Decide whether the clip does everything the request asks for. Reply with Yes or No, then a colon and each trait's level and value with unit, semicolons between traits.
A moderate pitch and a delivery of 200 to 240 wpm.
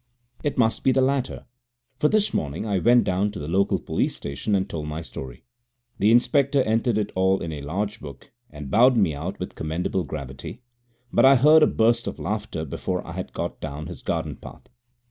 No: low, 100 Hz; fast, 205 wpm